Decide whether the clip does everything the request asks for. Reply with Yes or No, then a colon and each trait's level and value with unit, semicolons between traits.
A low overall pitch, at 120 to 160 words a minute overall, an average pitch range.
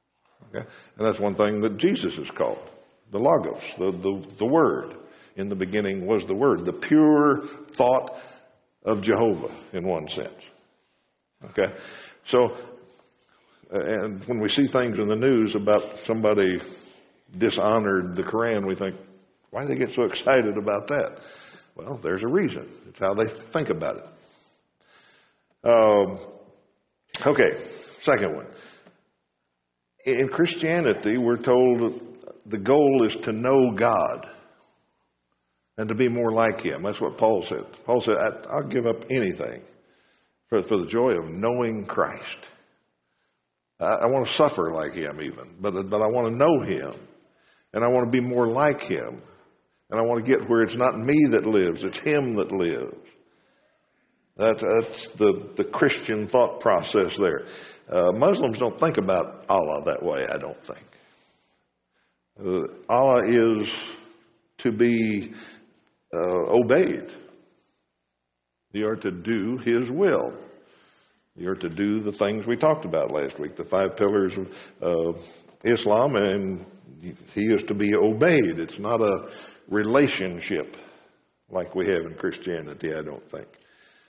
Yes: low, 110 Hz; average, 145 wpm; average, 4.7 semitones